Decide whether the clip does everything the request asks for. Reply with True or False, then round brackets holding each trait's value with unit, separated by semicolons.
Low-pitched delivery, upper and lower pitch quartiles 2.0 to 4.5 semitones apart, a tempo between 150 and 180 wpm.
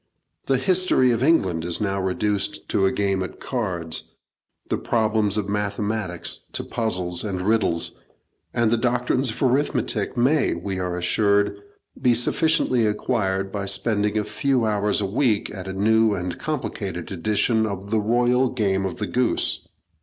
True (105 Hz; 3.7 semitones; 155 wpm)